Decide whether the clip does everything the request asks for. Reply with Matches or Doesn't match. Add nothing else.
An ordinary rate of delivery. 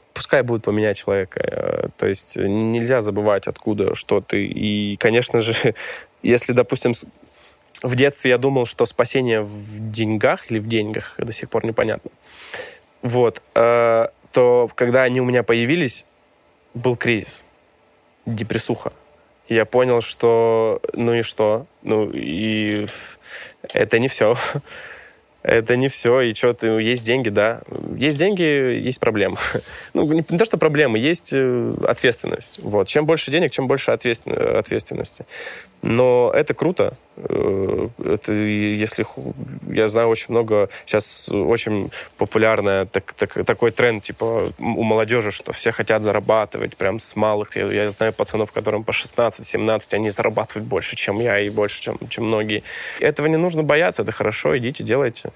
Matches